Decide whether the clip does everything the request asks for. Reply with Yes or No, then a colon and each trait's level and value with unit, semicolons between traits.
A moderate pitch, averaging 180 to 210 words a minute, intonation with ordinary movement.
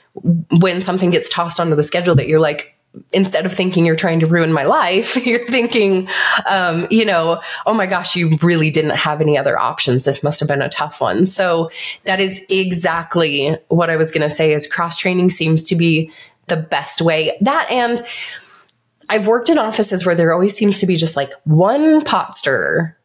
Yes: medium, 170 Hz; average, 200 wpm; average, 3.2 semitones